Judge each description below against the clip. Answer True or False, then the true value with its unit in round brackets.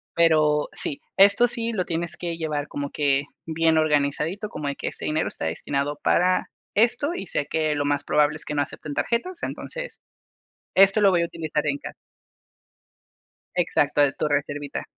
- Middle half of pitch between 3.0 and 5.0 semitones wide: True (4.0 semitones)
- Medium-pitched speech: True (155 Hz)